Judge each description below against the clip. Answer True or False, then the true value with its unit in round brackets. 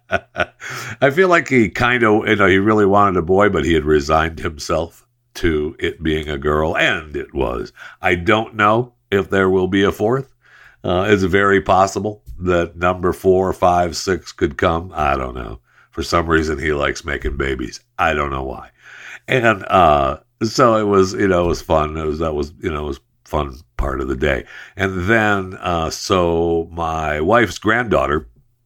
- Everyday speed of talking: True (190 wpm)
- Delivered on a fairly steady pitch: False (4.8 semitones)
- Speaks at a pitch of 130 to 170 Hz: False (90 Hz)